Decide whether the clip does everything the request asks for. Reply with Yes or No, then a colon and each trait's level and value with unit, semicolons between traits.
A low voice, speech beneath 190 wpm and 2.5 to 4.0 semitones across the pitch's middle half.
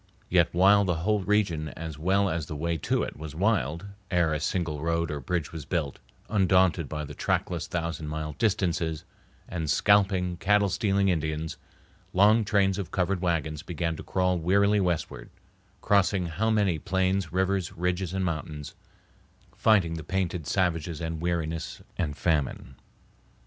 Yes: very low, 85 Hz; average, 155 wpm; average, 3.4 semitones